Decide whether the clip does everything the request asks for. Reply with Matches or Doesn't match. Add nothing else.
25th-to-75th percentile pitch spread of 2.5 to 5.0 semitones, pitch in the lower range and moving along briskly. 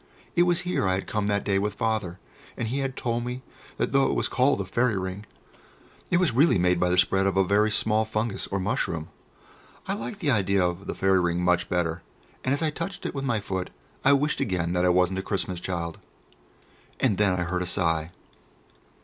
Doesn't match